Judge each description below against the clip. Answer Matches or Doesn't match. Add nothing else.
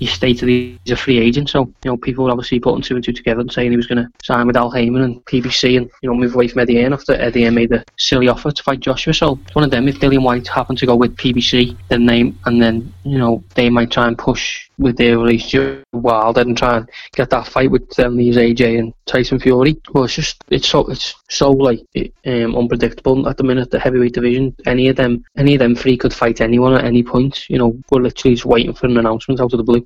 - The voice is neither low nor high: Doesn't match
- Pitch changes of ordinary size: Doesn't match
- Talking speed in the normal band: Doesn't match